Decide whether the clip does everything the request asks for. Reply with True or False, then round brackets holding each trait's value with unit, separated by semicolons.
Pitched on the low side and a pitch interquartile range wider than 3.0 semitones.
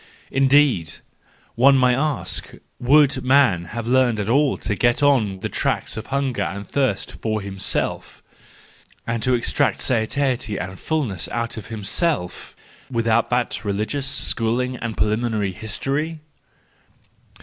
True (120 Hz; 4.2 semitones)